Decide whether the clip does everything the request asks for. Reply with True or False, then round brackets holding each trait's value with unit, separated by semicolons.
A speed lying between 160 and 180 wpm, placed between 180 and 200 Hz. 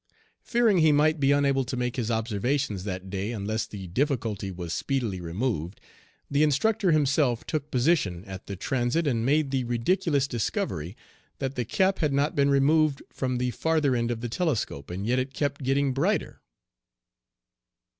False (165 wpm; 130 Hz)